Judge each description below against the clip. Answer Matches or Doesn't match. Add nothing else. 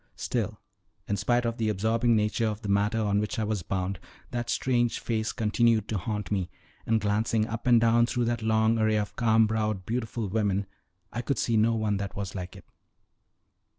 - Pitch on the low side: Matches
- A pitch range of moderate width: Doesn't match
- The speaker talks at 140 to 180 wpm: Doesn't match